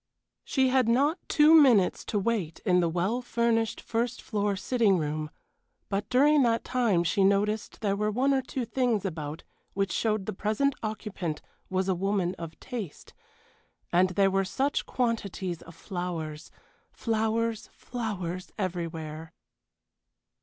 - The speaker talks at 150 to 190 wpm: No, average, 140 wpm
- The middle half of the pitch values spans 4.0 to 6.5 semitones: Yes, average, 4.5 semitones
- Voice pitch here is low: No, high, 205 Hz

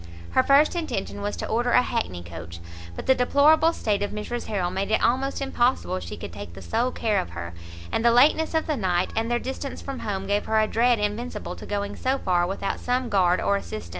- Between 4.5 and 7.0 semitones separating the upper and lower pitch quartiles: Yes, average, 5.0 semitones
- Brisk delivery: Yes, fast, 225 wpm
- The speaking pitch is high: Yes, high, 220 Hz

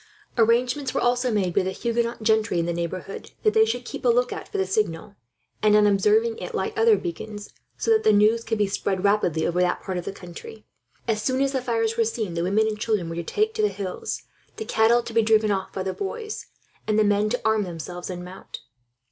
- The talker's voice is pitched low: No, high, 215 Hz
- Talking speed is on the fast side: Yes, fast, 235 wpm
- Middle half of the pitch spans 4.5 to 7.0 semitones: No, average, 4.1 semitones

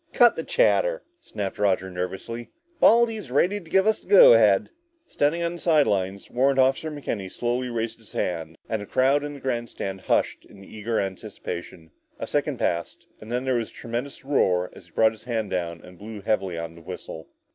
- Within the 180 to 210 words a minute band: Yes, average, 200 wpm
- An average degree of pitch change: No, wide, 6.7 semitones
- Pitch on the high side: No, low, 115 Hz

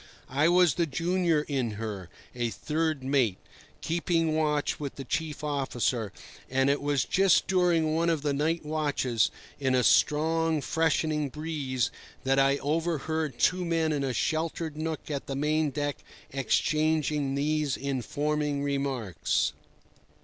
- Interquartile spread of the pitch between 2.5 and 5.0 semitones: Yes, average, 2.8 semitones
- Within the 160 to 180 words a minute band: No, average, 140 wpm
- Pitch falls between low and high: Yes, medium, 150 Hz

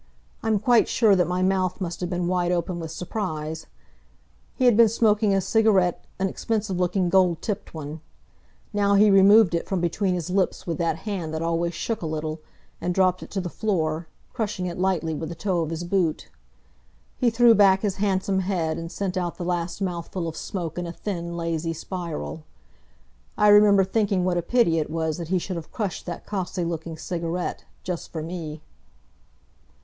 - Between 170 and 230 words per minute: Yes, average, 190 wpm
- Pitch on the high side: No, medium, 180 Hz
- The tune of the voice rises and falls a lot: No, average, 2.9 semitones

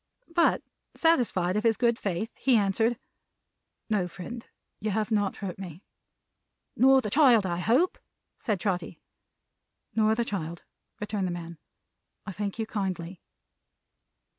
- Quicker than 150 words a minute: No, slow, 135 wpm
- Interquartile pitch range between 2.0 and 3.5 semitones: No, average, 4.1 semitones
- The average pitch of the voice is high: Yes, high, 210 Hz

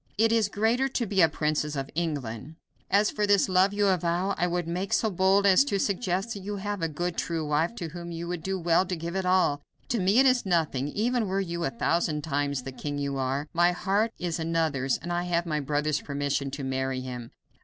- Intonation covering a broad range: No, average, 4.8 semitones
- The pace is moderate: No, fast, 230 wpm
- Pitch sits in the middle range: Yes, medium, 175 Hz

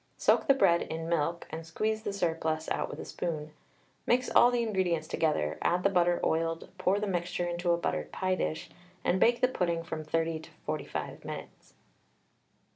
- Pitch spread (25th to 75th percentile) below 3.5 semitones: Yes, average, 2.8 semitones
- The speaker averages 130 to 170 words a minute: No, average, 185 wpm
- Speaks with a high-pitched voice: No, medium, 170 Hz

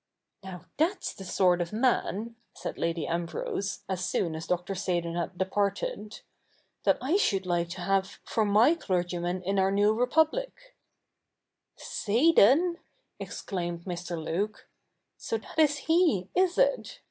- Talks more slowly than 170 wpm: Yes, average, 150 wpm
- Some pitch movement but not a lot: No, wide, 7.2 semitones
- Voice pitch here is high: Yes, high, 195 Hz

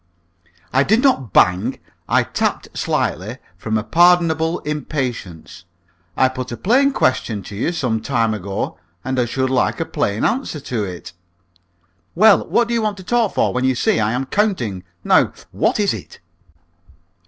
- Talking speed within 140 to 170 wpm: Yes, average, 165 wpm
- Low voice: Yes, low, 130 Hz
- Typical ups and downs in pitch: No, wide, 8.3 semitones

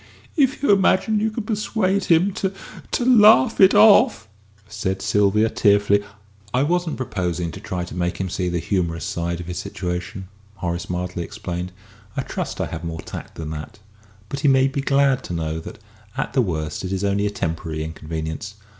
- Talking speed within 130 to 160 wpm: No, average, 185 wpm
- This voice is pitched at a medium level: No, low, 100 Hz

